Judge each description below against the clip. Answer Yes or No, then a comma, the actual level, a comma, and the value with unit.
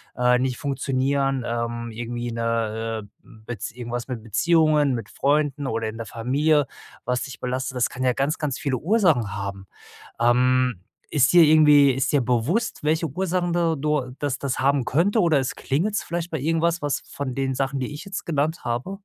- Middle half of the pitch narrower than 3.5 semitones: No, average, 4.0 semitones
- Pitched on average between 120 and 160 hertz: Yes, low, 135 Hz